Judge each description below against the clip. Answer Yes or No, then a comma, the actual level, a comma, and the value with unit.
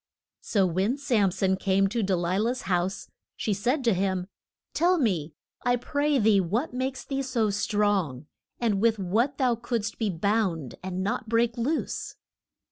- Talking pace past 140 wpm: Yes, average, 165 wpm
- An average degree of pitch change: Yes, average, 4.4 semitones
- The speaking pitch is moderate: No, high, 215 Hz